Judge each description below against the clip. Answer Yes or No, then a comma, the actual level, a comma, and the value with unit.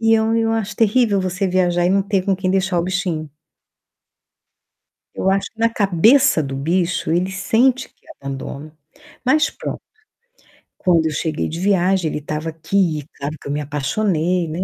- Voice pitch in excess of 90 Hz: Yes, medium, 185 Hz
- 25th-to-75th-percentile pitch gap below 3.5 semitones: No, average, 4.3 semitones